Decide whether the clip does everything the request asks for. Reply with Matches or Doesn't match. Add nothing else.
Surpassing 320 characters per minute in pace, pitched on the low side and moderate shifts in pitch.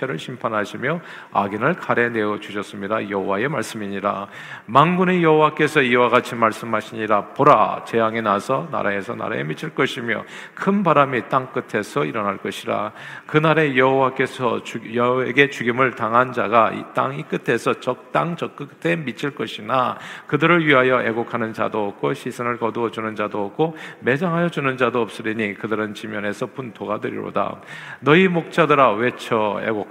Matches